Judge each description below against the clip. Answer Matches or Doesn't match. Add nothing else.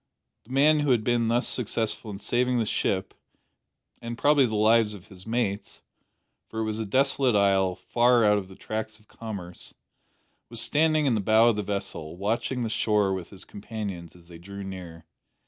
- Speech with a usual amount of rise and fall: Matches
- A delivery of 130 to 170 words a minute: Doesn't match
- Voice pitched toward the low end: Matches